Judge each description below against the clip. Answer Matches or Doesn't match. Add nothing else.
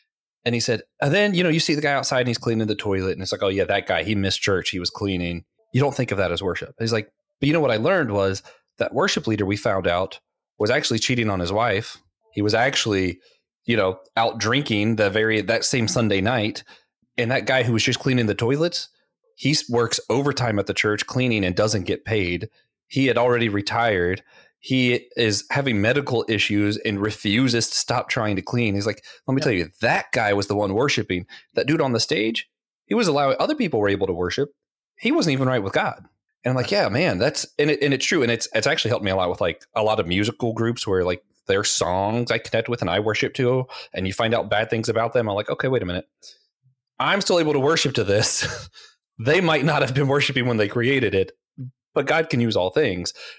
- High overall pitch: Doesn't match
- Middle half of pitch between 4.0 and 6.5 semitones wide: Matches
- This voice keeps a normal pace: Doesn't match